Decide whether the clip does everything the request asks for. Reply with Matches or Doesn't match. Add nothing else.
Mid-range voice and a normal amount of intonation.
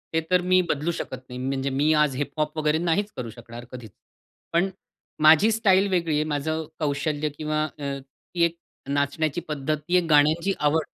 Matches